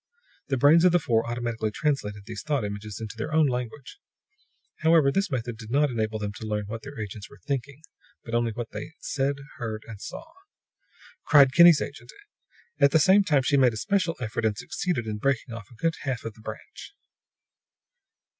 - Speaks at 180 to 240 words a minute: Yes, average, 190 wpm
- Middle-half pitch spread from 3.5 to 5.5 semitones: Yes, average, 5.0 semitones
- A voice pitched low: Yes, low, 125 Hz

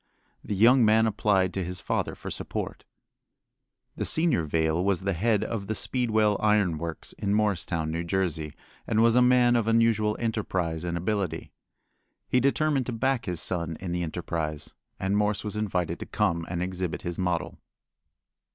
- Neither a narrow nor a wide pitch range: Yes, average, 4.5 semitones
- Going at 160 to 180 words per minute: Yes, average, 170 wpm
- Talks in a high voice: No, low, 100 Hz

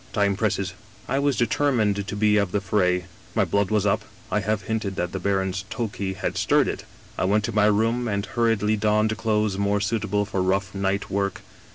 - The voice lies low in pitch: Yes, low, 105 Hz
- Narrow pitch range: Yes, narrow, 1.8 semitones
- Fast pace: Yes, fast, 210 wpm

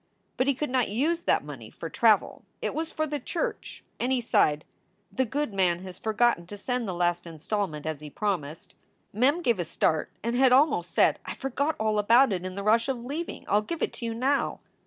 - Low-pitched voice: No, high, 225 Hz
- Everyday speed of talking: No, fast, 220 wpm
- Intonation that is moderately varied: No, wide, 6.3 semitones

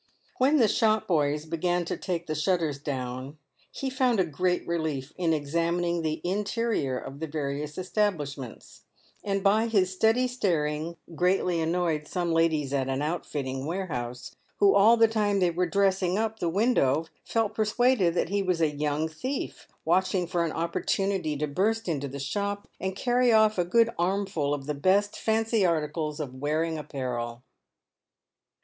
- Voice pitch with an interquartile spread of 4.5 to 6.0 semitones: Yes, average, 5.1 semitones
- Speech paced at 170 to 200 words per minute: Yes, average, 175 wpm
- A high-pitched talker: No, medium, 170 Hz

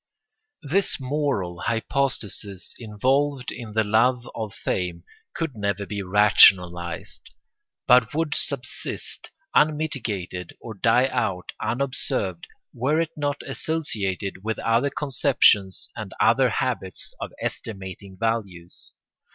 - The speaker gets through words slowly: Yes, slow, 105 wpm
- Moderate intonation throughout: No, wide, 6.1 semitones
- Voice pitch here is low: Yes, low, 115 Hz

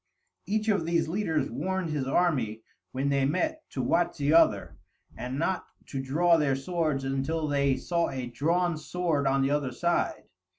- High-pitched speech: No, medium, 150 Hz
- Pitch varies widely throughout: No, average, 4.2 semitones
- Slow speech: No, average, 170 wpm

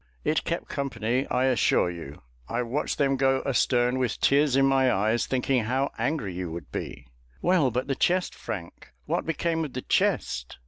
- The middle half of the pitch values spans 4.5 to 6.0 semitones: No, average, 3.7 semitones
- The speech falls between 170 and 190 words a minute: Yes, average, 180 wpm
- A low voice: Yes, low, 130 Hz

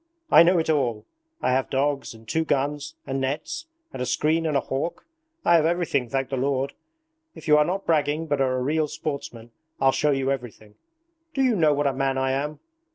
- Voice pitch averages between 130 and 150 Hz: Yes, medium, 140 Hz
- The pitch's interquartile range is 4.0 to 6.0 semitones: No, average, 2.9 semitones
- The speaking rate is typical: No, fast, 215 wpm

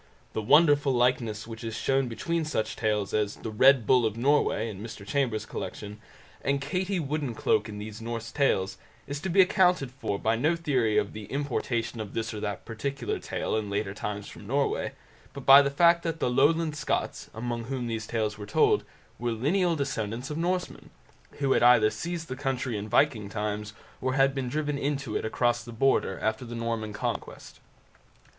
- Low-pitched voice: Yes, low, 120 Hz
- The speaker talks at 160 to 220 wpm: Yes, average, 190 wpm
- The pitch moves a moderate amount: Yes, average, 4.6 semitones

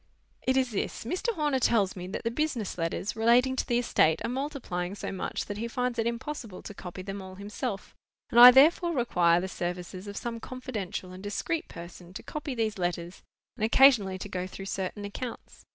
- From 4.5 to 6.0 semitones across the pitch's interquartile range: Yes, average, 5.2 semitones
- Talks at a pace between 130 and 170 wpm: No, average, 200 wpm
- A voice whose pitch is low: No, high, 215 Hz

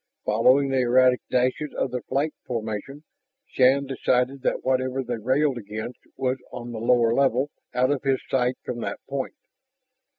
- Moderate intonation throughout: No, narrow, 1.9 semitones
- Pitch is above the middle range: No, low, 130 Hz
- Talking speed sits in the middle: Yes, average, 160 wpm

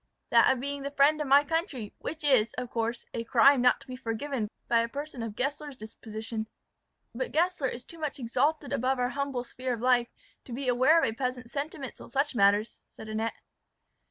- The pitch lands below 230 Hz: No, very high, 255 Hz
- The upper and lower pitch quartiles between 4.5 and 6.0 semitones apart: No, average, 3.5 semitones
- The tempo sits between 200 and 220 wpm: Yes, fast, 205 wpm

